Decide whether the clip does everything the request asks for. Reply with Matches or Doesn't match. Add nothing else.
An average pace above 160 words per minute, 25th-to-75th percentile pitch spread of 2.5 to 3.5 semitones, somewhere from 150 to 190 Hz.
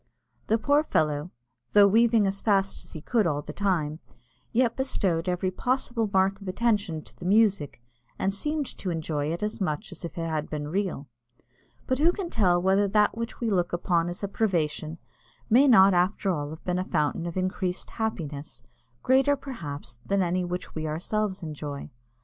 Doesn't match